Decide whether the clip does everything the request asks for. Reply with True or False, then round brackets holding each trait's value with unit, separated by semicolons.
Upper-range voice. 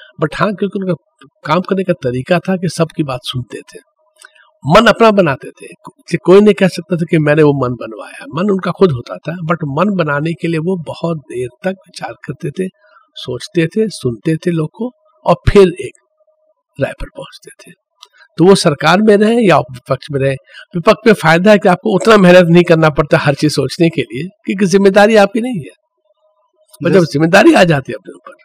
False (180 Hz)